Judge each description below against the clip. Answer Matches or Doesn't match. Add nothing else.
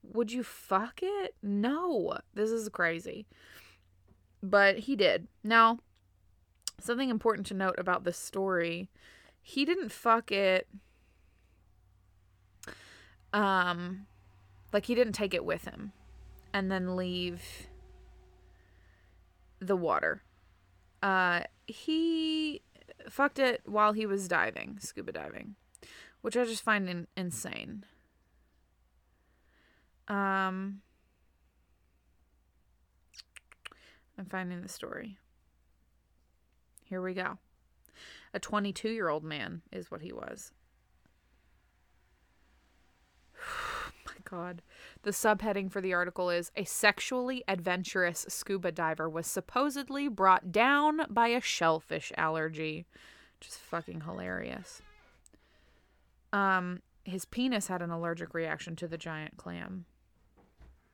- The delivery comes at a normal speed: Doesn't match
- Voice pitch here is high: Doesn't match